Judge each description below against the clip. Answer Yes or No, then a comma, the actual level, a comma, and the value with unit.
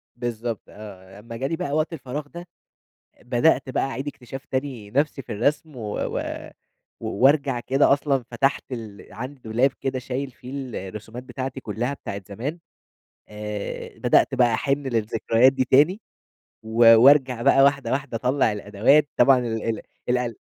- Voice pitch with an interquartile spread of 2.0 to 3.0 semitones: No, average, 3.4 semitones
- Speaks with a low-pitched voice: Yes, low, 125 Hz